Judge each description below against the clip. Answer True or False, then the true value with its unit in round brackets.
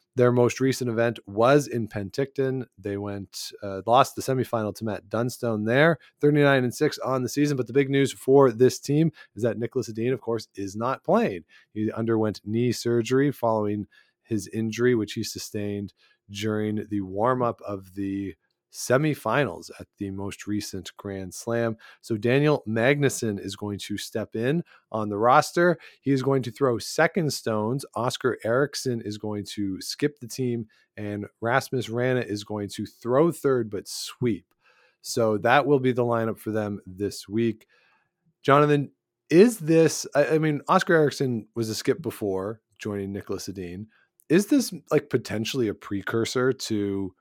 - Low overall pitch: True (115 Hz)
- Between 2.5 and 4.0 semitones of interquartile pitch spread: False (4.6 semitones)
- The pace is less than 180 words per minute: True (165 wpm)